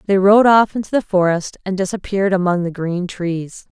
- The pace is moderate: Yes, average, 190 wpm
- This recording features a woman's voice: Yes, female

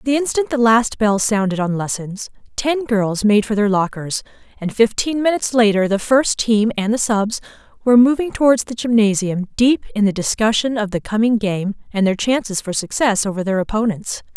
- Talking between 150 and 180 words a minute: No, average, 190 wpm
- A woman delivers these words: Yes, female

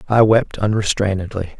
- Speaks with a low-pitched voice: Yes, low, 105 Hz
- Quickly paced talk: No, slow, 115 wpm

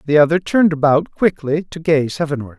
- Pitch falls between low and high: Yes, medium, 150 Hz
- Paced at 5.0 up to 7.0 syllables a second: Yes, 5.8 syllables/s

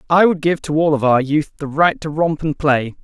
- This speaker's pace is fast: Yes, fast, 275 wpm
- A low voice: No, medium, 155 Hz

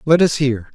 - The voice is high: No, medium, 140 Hz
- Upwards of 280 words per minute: No, fast, 240 wpm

